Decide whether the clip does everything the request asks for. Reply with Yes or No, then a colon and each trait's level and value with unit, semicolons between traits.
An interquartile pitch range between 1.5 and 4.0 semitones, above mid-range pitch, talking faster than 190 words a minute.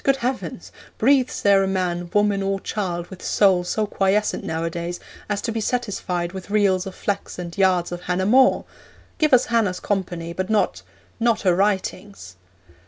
No: average, 2.9 semitones; high, 195 Hz; average, 170 wpm